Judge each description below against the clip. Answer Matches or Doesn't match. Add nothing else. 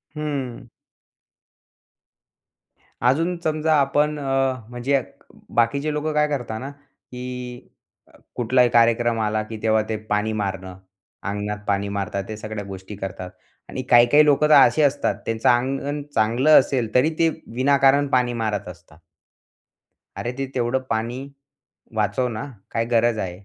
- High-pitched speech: Doesn't match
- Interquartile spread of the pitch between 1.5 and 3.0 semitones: Doesn't match